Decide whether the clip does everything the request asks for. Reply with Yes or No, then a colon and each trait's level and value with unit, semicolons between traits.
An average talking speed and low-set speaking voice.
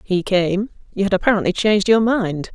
No: average, 190 wpm; high, 200 Hz